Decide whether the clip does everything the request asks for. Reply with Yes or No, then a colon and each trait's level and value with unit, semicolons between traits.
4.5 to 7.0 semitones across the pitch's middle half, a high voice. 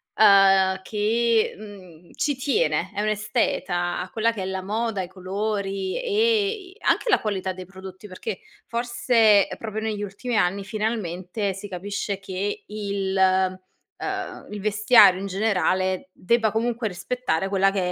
No: average, 2.7 semitones; high, 200 Hz